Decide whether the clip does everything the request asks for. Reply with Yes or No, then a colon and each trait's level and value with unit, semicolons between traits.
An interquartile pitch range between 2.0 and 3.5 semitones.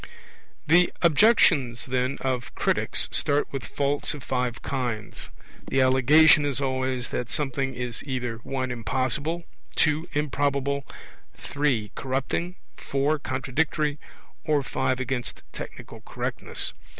Yes: narrow, 2.6 semitones